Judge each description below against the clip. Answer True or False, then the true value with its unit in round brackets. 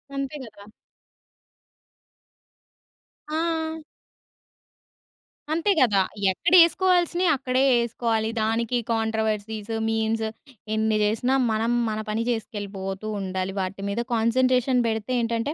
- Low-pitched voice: False (225 Hz)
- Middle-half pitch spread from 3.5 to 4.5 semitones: False (3.0 semitones)